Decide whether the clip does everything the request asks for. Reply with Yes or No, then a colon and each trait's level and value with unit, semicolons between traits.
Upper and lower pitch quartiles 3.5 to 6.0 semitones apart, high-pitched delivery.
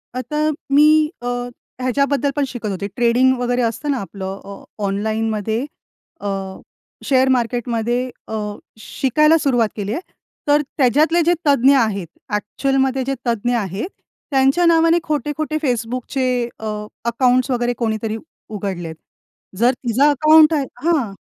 Yes: average, 4.2 semitones; very high, 250 Hz